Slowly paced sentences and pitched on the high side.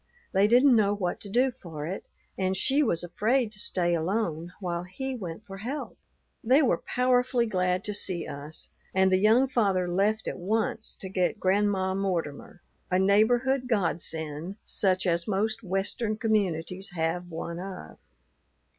No: average, 155 wpm; high, 195 Hz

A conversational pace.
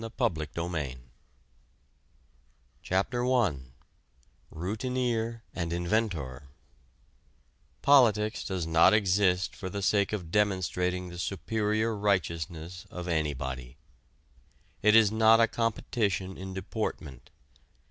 No: slow, 100 wpm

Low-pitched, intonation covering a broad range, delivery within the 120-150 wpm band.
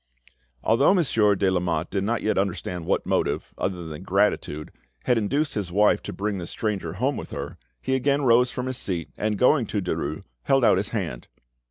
No: low, 105 Hz; wide, 5.7 semitones; average, 195 wpm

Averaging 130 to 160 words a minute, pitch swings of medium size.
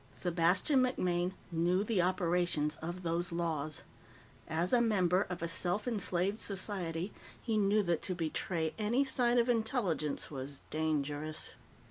Yes: slow, 135 wpm; average, 4.1 semitones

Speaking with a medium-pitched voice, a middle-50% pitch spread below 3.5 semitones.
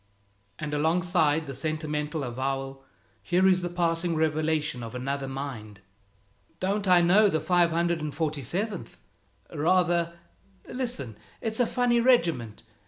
No: medium, 160 Hz; average, 4.2 semitones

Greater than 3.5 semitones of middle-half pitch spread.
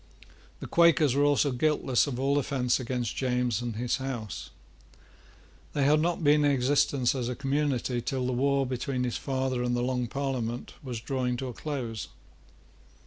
No: narrow, 2.4 semitones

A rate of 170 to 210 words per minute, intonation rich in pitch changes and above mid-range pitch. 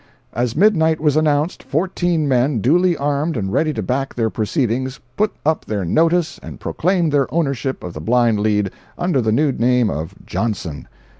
No: average, 180 wpm; wide, 6.0 semitones; low, 135 Hz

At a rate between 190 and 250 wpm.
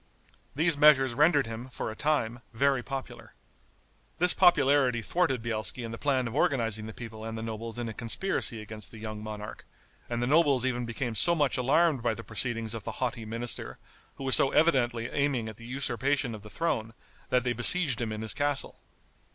Yes: average, 195 wpm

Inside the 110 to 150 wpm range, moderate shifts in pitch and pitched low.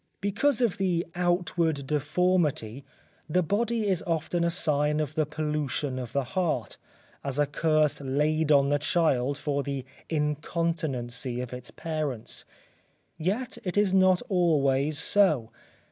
No: slow, 135 wpm; average, 4.0 semitones; medium, 155 Hz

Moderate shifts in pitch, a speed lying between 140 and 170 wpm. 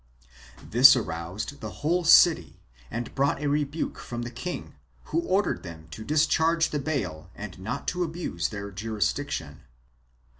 No: wide, 7.7 semitones; average, 145 wpm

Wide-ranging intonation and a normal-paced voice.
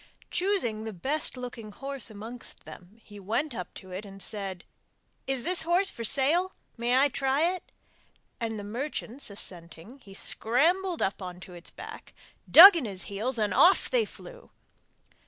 Yes: wide, 7.1 semitones; average, 160 wpm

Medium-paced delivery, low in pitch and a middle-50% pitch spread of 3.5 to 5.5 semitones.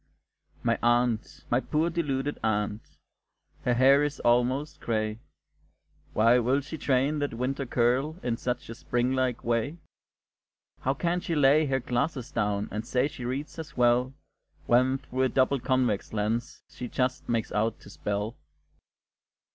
No: average, 150 wpm; low, 125 Hz; average, 2.8 semitones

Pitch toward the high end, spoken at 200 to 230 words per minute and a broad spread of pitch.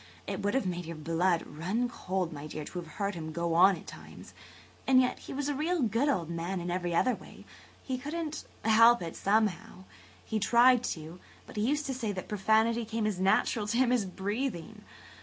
Yes: high, 205 Hz; fast, 205 wpm; wide, 6.0 semitones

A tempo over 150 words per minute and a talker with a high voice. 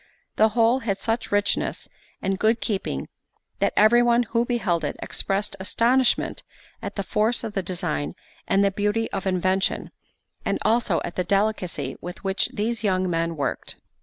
Yes: average, 160 wpm; high, 200 Hz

